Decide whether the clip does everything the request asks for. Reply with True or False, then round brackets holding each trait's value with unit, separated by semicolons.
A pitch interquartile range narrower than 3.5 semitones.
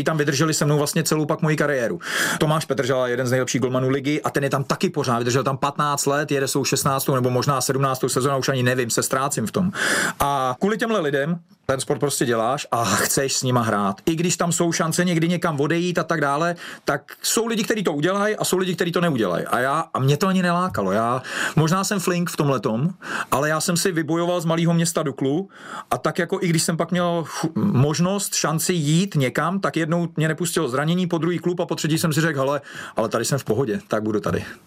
False (4.3 semitones)